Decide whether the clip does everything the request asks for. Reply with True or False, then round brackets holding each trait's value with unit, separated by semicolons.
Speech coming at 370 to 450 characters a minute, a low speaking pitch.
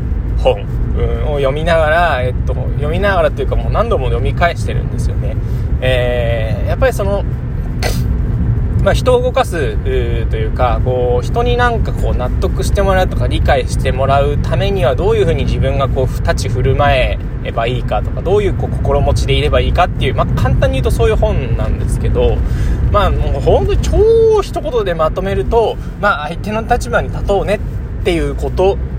True (375 characters per minute; 120 Hz)